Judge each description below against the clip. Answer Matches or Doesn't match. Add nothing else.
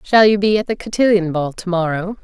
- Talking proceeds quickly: Matches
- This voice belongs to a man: Doesn't match